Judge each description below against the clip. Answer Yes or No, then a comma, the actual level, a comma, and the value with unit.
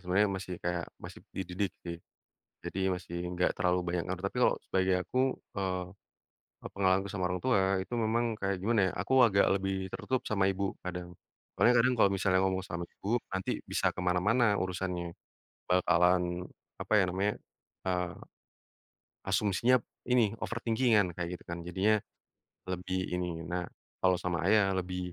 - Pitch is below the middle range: Yes, very low, 95 Hz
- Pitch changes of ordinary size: No, narrow, 2.0 semitones